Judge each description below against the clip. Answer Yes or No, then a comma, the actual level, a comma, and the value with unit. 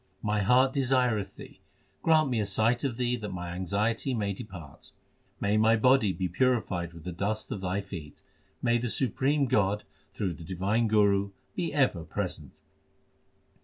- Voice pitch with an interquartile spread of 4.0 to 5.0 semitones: Yes, average, 4.5 semitones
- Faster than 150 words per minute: Yes, average, 165 wpm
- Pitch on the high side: No, low, 105 Hz